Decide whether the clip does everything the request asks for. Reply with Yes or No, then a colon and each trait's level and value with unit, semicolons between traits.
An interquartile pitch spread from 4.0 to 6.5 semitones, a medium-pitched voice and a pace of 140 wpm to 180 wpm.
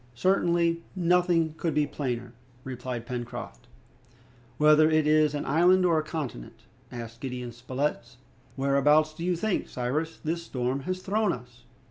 Yes: average, 5.1 semitones; medium, 150 Hz; average, 145 wpm